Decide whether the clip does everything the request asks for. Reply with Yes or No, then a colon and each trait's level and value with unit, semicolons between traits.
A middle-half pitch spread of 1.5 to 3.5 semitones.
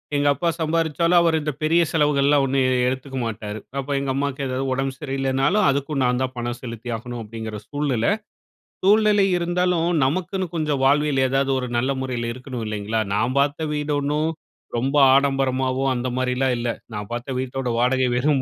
Yes: average, 2.8 semitones